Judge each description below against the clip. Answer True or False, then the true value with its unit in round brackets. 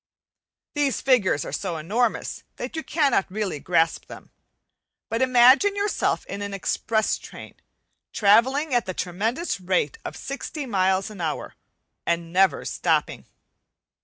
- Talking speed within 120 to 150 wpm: True (135 wpm)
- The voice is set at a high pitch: True (210 Hz)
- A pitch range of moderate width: False (5.9 semitones)